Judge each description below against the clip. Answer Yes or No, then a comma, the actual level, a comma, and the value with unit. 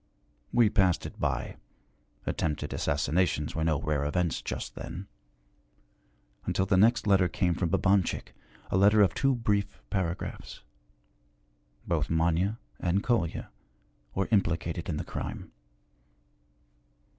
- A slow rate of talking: Yes, slow, 120 wpm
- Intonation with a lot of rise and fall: No, average, 3.5 semitones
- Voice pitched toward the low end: Yes, very low, 90 Hz